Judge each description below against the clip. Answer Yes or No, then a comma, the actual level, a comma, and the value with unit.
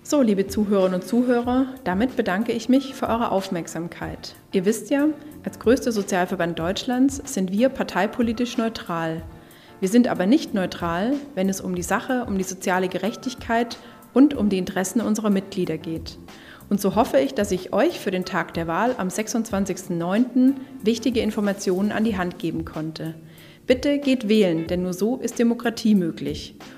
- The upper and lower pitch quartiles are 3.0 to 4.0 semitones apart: No, average, 5.0 semitones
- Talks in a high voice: Yes, high, 205 Hz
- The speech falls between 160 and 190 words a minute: Yes, average, 165 wpm